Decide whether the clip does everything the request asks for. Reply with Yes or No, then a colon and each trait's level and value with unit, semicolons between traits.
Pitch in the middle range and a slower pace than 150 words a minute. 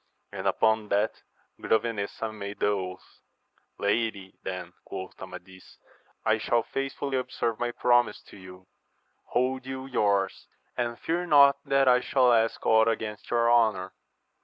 No: low, 110 Hz; average, 140 wpm